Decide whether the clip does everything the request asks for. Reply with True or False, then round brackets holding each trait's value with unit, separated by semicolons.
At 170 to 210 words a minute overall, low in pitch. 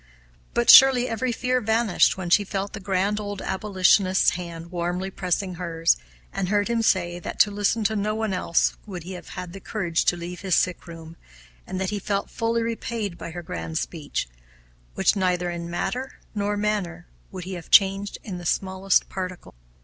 False (185 wpm; 190 Hz)